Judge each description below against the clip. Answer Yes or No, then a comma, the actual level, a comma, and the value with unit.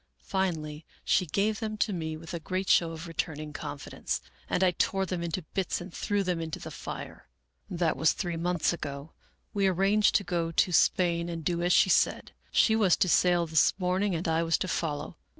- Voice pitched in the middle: Yes, medium, 175 Hz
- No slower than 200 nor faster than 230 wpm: Yes, fast, 205 wpm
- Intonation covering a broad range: No, narrow, 2.6 semitones